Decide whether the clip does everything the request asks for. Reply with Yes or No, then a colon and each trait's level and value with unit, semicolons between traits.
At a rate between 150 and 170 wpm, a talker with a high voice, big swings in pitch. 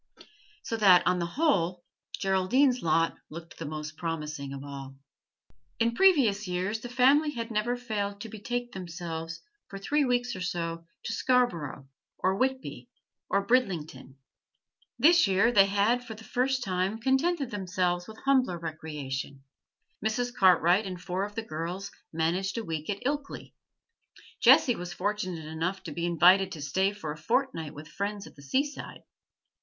Yes: average, 155 wpm; high, 195 Hz; wide, 6.1 semitones